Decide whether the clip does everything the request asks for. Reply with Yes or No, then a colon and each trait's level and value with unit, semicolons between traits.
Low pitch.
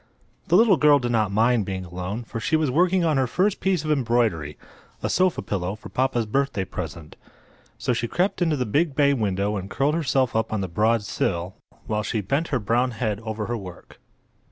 Yes: low, 115 Hz